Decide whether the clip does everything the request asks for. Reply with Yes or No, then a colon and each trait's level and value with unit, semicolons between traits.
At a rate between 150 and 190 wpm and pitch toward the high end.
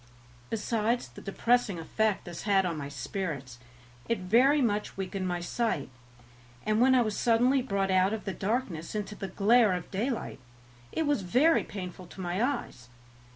Yes: average, 165 wpm; high, 205 Hz